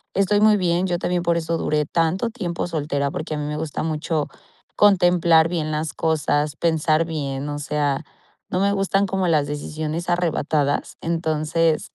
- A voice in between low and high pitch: Yes, medium, 160 Hz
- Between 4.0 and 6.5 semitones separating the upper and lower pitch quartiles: No, narrow, 2.6 semitones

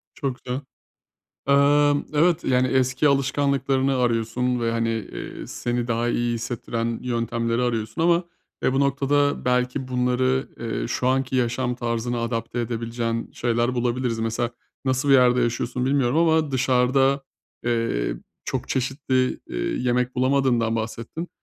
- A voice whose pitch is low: Yes, low, 125 Hz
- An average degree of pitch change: No, narrow, 2.3 semitones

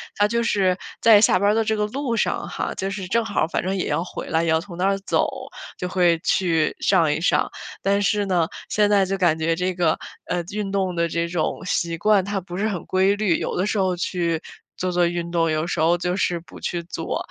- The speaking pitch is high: No, medium, 180 Hz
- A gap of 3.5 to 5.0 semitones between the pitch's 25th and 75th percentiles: No, average, 3.0 semitones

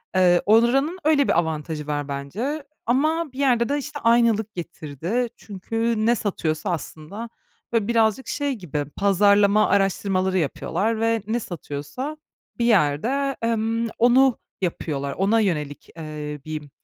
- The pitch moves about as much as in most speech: No, wide, 6.7 semitones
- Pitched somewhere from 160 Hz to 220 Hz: Yes, high, 210 Hz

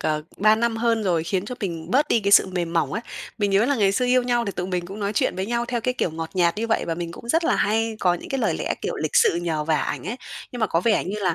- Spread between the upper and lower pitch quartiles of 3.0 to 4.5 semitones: No, average, 5.0 semitones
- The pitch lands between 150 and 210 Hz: Yes, high, 200 Hz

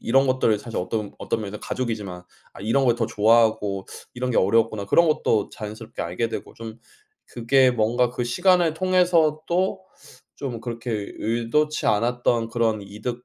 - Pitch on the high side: No, low, 115 Hz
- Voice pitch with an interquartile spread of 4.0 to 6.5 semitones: No, average, 3.2 semitones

